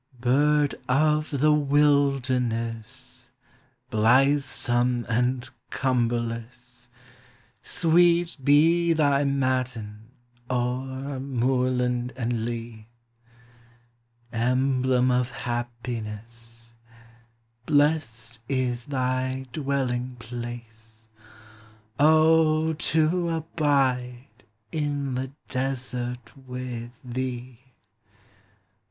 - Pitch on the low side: Yes, low, 125 Hz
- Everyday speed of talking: No, slow, 65 wpm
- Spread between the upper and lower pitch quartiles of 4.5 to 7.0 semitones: No, average, 2.8 semitones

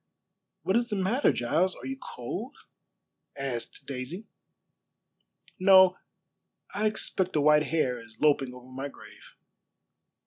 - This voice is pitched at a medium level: Yes, medium, 160 Hz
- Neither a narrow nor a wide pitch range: No, wide, 7.1 semitones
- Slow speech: Yes, slow, 125 wpm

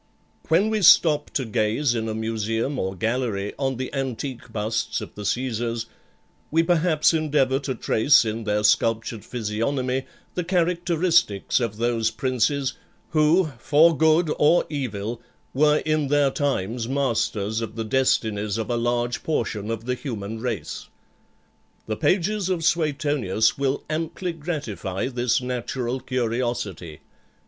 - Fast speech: No, slow, 135 wpm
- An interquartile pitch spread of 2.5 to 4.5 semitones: No, average, 5.1 semitones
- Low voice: Yes, low, 125 Hz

